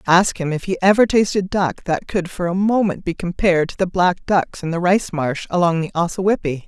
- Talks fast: Yes, fast, 225 wpm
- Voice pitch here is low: No, medium, 180 Hz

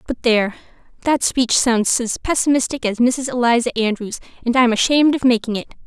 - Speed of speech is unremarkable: Yes, average, 175 wpm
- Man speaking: No, female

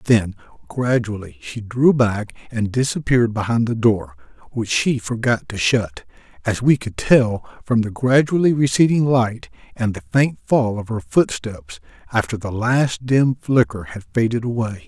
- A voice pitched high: No, low, 115 Hz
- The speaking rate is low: No, average, 155 wpm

